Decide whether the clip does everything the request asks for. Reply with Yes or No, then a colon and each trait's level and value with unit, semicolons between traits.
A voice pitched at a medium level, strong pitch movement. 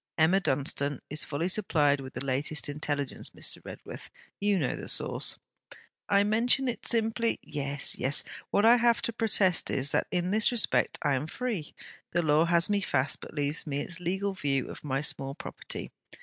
Yes: medium, 160 Hz; wide, 6.2 semitones